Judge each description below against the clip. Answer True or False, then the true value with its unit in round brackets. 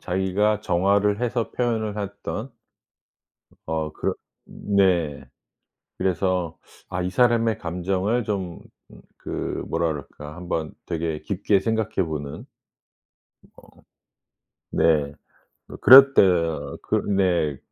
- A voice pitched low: True (95 Hz)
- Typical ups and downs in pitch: True (4.2 semitones)